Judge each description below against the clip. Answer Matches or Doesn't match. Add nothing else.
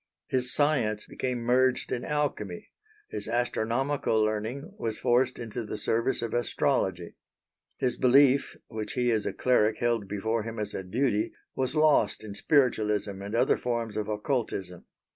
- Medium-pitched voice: Doesn't match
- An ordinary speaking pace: Matches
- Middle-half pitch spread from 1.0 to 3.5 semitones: Matches